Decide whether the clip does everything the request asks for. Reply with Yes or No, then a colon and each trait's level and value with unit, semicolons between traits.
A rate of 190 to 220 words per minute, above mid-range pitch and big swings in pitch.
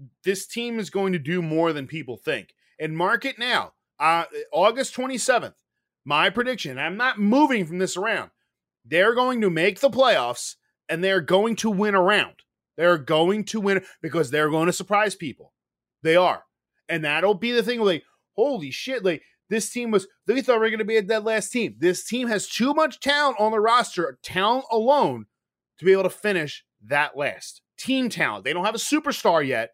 Yes: average, 200 wpm; high, 200 Hz; wide, 6.0 semitones